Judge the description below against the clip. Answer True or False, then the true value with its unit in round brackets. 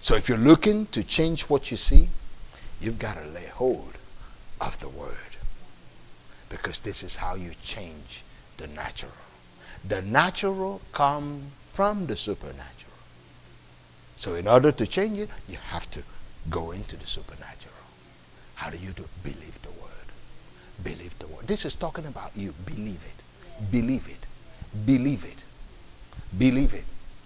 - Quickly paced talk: False (150 wpm)